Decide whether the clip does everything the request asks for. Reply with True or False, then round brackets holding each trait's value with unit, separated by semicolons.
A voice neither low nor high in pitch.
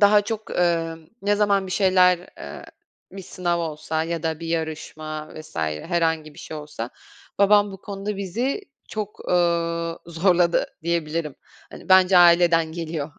True (170 Hz)